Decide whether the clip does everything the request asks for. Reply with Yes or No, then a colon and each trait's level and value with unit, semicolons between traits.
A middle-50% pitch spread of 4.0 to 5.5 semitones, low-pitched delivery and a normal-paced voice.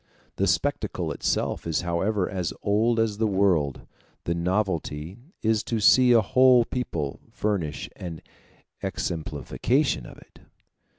No: average, 5.0 semitones; low, 100 Hz; slow, 125 wpm